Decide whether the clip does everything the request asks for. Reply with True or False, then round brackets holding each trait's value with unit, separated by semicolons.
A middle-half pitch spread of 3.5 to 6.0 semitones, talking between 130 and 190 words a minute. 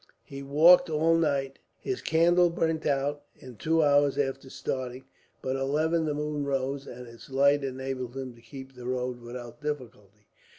False (2.7 semitones; 170 wpm)